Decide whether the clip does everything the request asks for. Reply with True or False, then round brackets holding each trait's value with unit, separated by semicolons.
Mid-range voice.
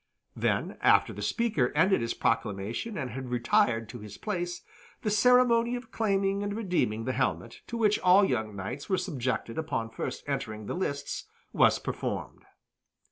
True (150 Hz)